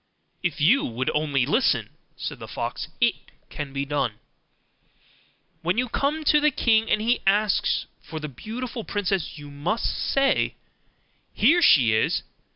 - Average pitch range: No, wide, 8.7 semitones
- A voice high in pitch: Yes, high, 195 Hz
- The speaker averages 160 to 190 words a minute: No, average, 150 wpm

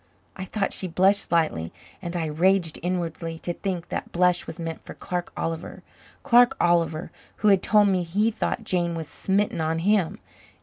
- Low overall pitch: No, medium, 175 Hz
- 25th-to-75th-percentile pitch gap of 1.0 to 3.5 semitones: Yes, average, 3.0 semitones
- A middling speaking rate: Yes, average, 175 wpm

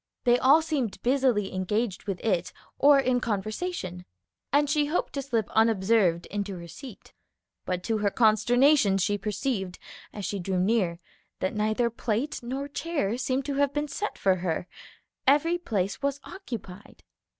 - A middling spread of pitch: No, wide, 6.1 semitones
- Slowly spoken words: No, average, 155 wpm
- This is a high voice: Yes, high, 225 Hz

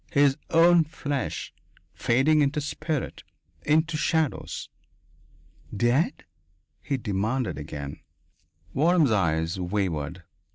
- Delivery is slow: Yes, slow, 85 wpm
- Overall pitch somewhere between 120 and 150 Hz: Yes, low, 135 Hz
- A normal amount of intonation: No, wide, 8.3 semitones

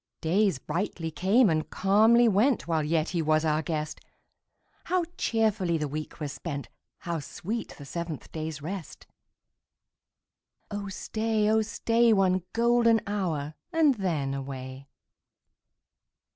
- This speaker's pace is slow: Yes, slow, 125 wpm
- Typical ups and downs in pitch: No, wide, 6.0 semitones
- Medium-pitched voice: Yes, medium, 175 Hz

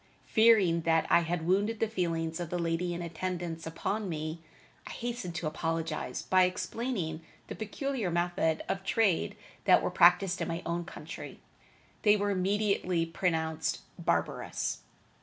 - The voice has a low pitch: No, medium, 175 Hz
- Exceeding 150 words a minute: No, average, 145 wpm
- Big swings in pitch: No, average, 3.4 semitones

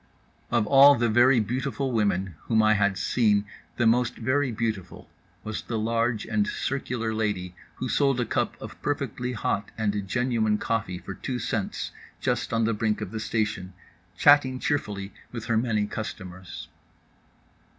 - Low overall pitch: Yes, low, 110 Hz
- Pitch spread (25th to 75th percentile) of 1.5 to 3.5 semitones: Yes, average, 2.9 semitones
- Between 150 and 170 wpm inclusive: Yes, average, 155 wpm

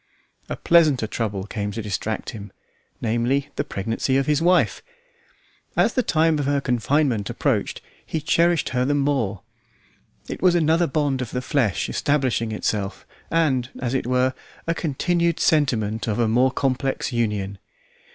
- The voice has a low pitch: Yes, low, 130 Hz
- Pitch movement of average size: Yes, average, 4.9 semitones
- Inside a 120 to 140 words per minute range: No, average, 150 wpm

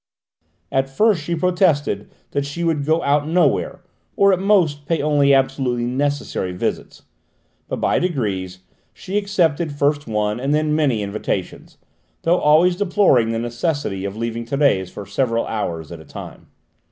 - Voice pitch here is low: No, medium, 145 Hz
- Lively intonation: Yes, wide, 6.3 semitones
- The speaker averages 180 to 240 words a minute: No, average, 155 wpm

